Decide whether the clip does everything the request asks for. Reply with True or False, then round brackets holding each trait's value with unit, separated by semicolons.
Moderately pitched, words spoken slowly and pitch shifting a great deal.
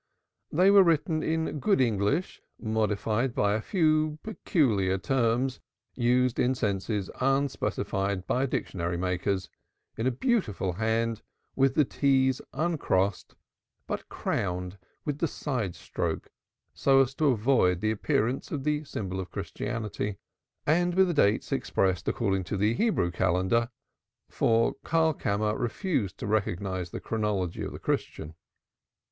False (115 Hz; 130 wpm; 6.3 semitones)